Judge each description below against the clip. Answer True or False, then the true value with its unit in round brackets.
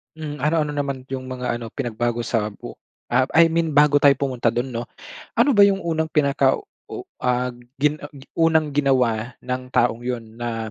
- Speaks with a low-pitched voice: True (130 Hz)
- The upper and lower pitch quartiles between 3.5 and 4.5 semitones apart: True (3.8 semitones)